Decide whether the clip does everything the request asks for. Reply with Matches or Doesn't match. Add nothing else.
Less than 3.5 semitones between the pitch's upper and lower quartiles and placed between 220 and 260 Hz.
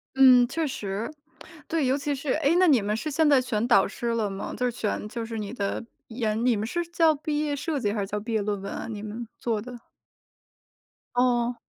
Doesn't match